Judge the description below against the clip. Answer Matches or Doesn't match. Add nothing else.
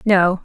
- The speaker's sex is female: Matches